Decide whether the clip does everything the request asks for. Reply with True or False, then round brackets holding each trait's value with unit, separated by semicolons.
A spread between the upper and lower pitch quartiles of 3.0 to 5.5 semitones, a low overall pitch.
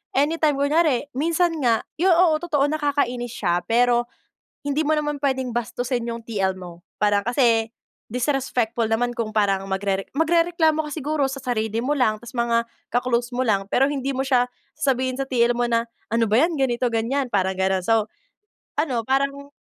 False (3.9 semitones; 250 Hz)